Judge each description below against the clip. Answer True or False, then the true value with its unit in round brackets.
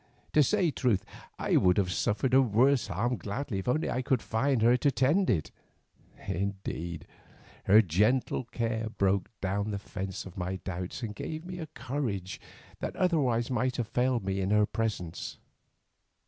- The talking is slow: False (165 wpm)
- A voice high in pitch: False (110 Hz)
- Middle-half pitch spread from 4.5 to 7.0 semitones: True (5.1 semitones)